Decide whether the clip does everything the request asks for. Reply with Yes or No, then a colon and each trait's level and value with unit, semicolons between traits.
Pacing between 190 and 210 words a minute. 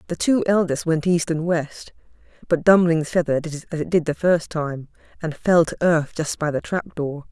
Yes: fast, 205 wpm